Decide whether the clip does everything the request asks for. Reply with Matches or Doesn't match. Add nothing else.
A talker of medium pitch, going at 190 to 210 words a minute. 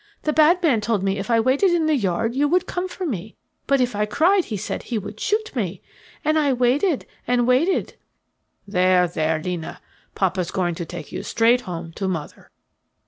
Doesn't match